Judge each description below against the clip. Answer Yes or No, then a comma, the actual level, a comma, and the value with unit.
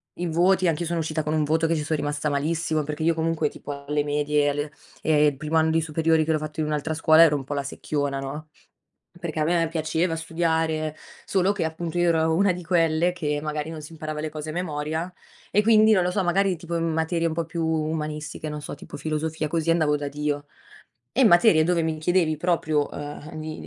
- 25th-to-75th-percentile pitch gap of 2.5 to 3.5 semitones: No, narrow, 1.7 semitones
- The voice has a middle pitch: Yes, medium, 160 Hz